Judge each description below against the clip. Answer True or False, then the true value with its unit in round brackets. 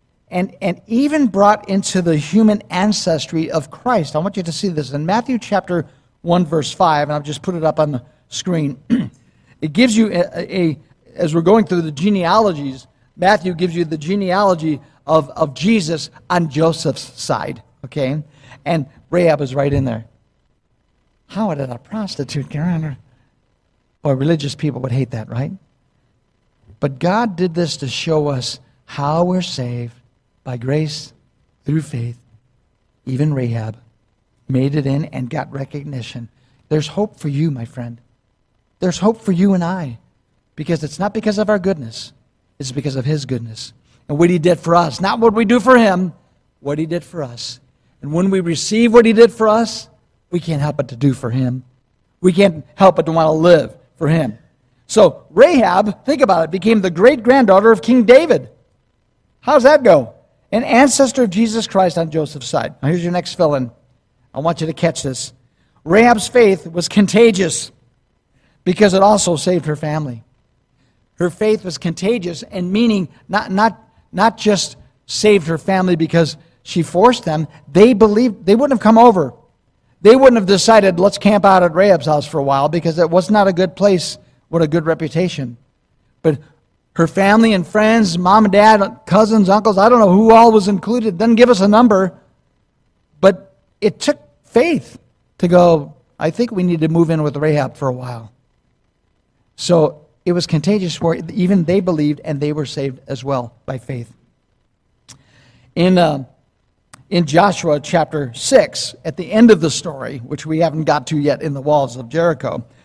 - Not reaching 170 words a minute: False (180 wpm)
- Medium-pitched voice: True (160 Hz)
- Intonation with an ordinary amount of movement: False (6.4 semitones)